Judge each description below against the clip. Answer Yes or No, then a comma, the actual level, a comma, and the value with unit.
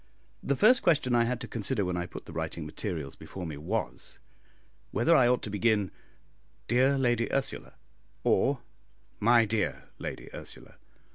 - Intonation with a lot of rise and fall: Yes, wide, 5.8 semitones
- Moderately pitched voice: No, low, 115 Hz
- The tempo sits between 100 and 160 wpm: Yes, average, 155 wpm